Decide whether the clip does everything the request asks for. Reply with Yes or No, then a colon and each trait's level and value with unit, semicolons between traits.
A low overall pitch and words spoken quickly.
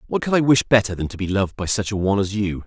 Yes: low, 100 Hz; fast, 340 wpm